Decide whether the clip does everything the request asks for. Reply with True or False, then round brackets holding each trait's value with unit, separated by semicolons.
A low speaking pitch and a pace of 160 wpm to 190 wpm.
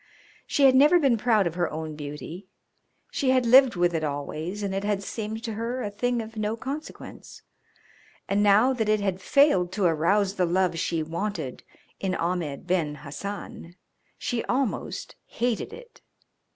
False (200 Hz; 165 wpm)